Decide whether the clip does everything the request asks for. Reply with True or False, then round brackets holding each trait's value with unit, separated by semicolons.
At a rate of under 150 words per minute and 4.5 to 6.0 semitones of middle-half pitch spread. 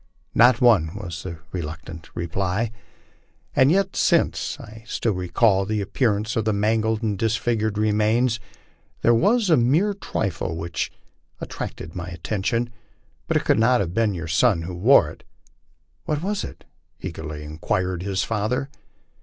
False (155 wpm; 4.8 semitones)